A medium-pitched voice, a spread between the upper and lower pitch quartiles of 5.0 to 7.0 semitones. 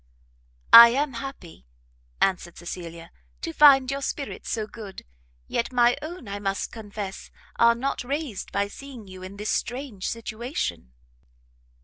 No: high, 230 Hz; wide, 5.6 semitones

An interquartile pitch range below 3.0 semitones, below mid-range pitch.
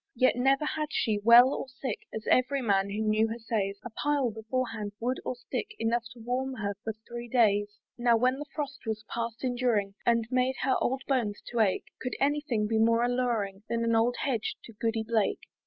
No: narrow, 2.6 semitones; high, 235 Hz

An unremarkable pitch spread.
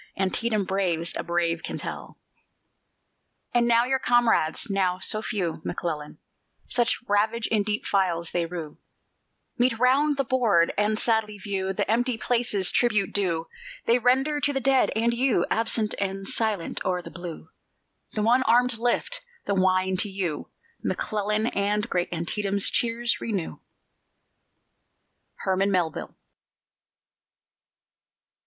Yes: average, 4.1 semitones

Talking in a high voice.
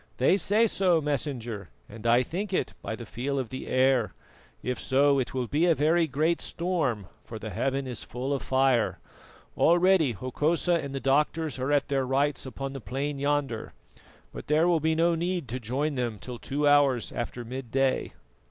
No: low, 135 Hz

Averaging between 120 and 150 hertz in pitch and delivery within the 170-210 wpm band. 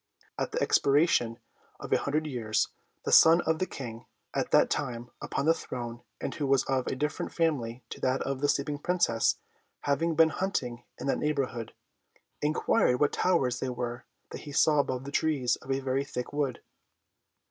Yes: low, 135 Hz; average, 180 wpm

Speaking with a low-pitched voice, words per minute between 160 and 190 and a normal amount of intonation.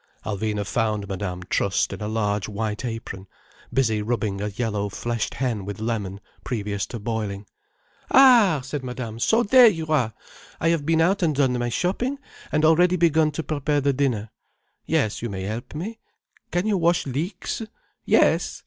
No: low, 120 Hz; average, 165 wpm; wide, 7.4 semitones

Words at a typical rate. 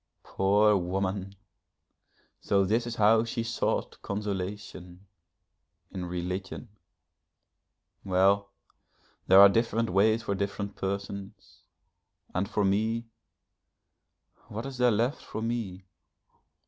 No: slow, 100 wpm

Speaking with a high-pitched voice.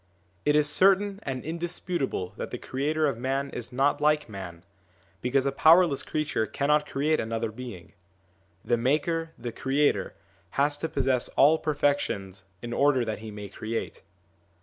No: medium, 140 Hz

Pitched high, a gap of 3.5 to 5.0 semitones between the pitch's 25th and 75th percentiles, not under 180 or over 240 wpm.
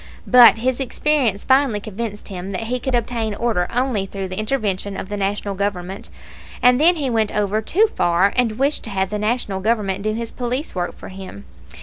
Yes: high, 215 Hz; average, 4.0 semitones; average, 200 wpm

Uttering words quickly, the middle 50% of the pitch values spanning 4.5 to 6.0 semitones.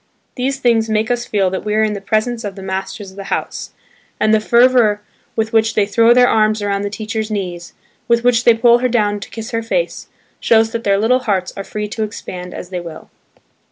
No: fast, 230 wpm; narrow, 2.6 semitones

